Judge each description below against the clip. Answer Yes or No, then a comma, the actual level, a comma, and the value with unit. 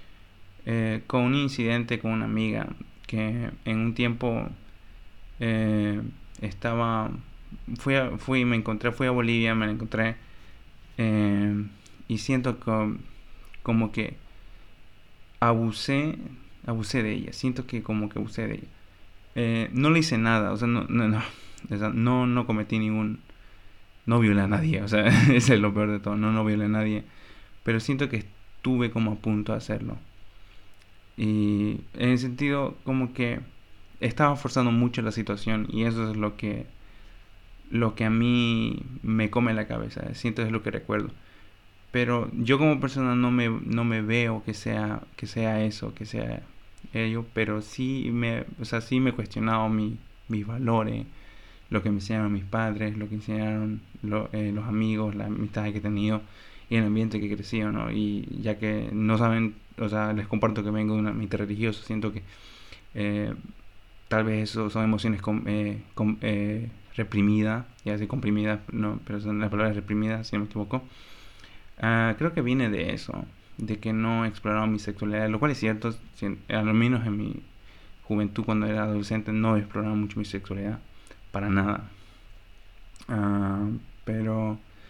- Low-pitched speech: Yes, low, 110 Hz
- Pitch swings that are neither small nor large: No, narrow, 1.8 semitones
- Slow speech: No, average, 170 wpm